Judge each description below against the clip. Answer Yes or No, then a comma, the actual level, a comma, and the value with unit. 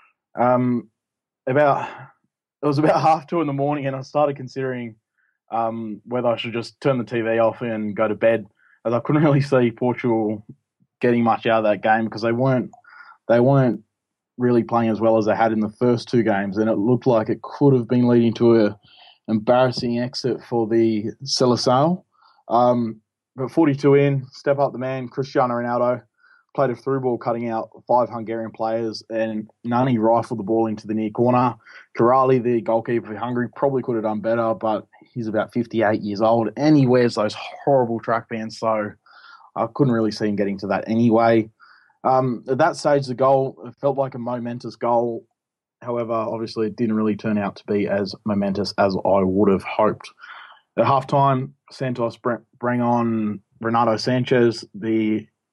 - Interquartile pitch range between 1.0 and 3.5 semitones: Yes, narrow, 2.5 semitones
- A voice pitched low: Yes, low, 120 Hz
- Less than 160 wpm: No, average, 185 wpm